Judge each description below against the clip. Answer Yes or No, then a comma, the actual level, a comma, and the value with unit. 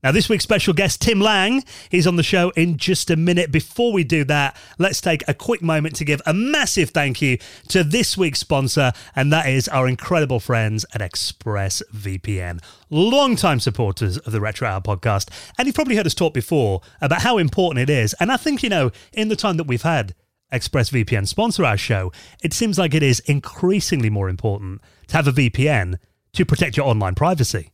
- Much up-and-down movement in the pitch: Yes, wide, 8.6 semitones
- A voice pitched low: No, medium, 145 Hz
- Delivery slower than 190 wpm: No, average, 200 wpm